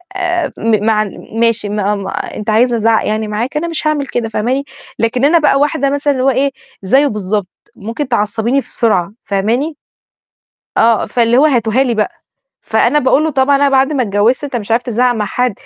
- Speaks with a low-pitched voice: No, high, 240 Hz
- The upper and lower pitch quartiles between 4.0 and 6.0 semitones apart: Yes, average, 4.3 semitones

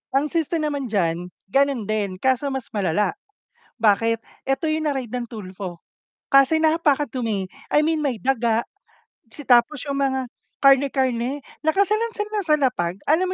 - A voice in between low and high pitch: No, very high, 265 Hz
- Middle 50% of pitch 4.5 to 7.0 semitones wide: Yes, average, 5.0 semitones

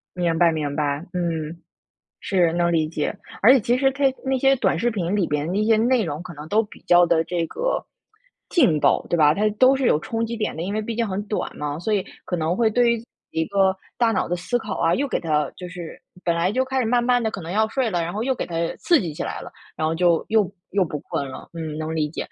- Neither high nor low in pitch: Yes, medium, 180 Hz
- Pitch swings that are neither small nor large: No, wide, 5.9 semitones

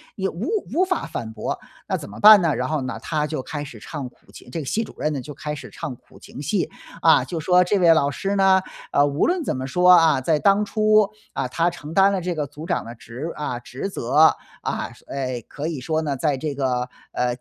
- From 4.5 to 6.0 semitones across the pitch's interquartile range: Yes, average, 5.3 semitones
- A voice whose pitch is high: No, medium, 155 Hz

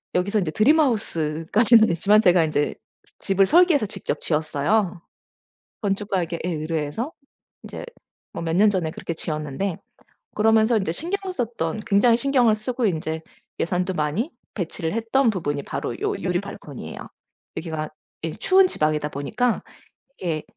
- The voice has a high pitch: Yes, high, 195 Hz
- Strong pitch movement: Yes, wide, 6.0 semitones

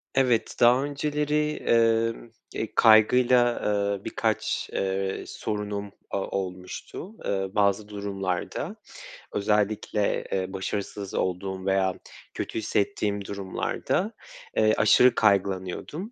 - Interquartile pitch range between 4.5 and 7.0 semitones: No, average, 3.1 semitones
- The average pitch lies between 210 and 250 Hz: No, low, 105 Hz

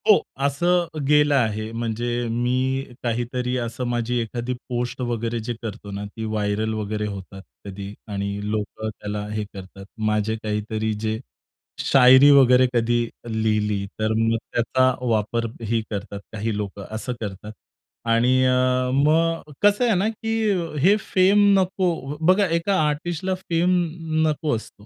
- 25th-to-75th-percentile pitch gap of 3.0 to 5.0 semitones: No, wide, 5.4 semitones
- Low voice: Yes, low, 120 Hz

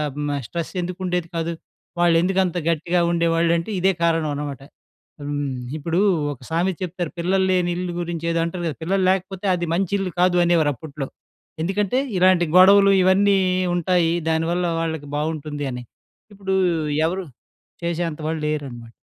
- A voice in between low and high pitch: Yes, medium, 170 Hz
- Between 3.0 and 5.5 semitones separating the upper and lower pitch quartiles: No, narrow, 2.5 semitones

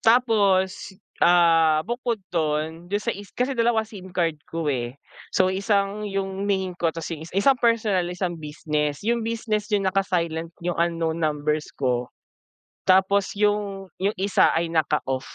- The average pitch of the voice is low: No, medium, 185 Hz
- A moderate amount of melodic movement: Yes, average, 4.0 semitones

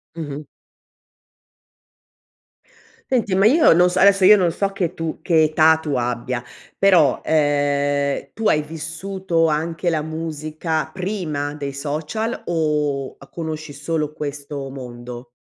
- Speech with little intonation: No, average, 3.3 semitones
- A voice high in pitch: No, medium, 155 Hz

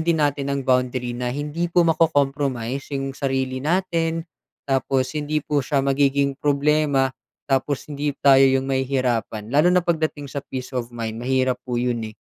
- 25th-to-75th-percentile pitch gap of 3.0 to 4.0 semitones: No, narrow, 2.4 semitones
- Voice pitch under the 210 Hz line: Yes, low, 135 Hz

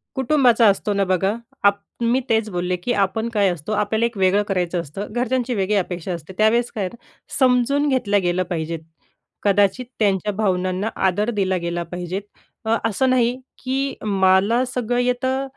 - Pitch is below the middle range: No, high, 205 Hz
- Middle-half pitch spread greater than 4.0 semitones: Yes, average, 4.5 semitones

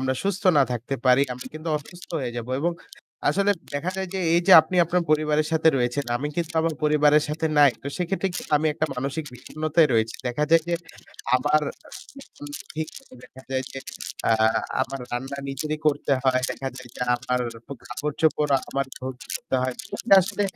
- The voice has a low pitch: No, medium, 150 Hz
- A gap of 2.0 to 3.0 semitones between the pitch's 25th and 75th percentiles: No, average, 3.5 semitones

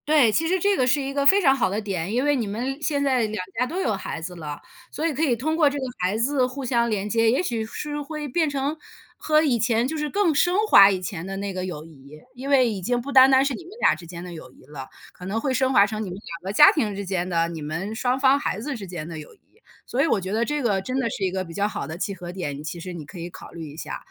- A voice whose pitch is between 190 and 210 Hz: No, high, 225 Hz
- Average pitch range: No, wide, 7.2 semitones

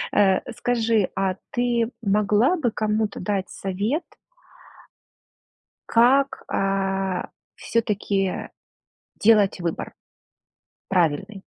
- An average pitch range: Yes, average, 3.0 semitones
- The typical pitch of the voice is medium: No, high, 205 Hz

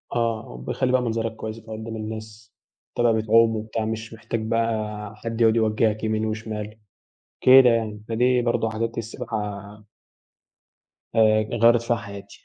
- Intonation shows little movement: Yes, narrow, 1.1 semitones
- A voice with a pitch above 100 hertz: Yes, low, 110 Hz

